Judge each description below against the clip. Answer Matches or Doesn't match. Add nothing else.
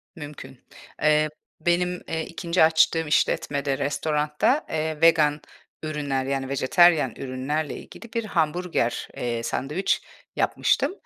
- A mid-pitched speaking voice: Matches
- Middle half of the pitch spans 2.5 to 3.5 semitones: Matches